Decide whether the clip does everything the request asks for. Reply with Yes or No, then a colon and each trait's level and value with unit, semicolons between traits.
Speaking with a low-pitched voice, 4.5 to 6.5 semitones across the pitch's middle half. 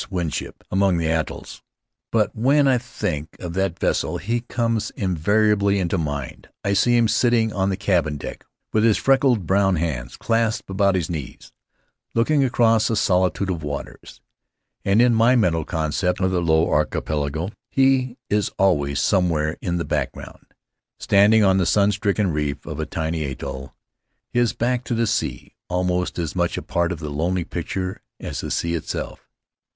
Yes: very low, 95 Hz; average, 5.3 semitones